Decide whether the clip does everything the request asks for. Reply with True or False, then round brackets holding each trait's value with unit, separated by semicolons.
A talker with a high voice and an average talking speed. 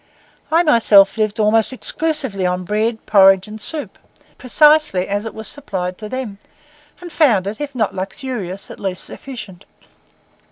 True (215 Hz; 150 wpm)